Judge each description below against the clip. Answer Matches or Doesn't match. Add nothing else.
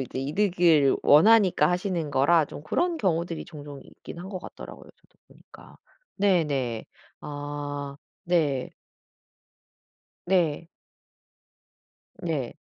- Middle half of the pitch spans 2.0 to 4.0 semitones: Matches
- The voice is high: Doesn't match